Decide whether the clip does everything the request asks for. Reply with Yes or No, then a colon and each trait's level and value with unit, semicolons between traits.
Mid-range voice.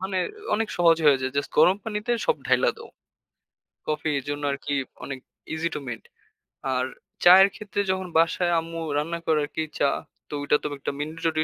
Yes: medium, 165 Hz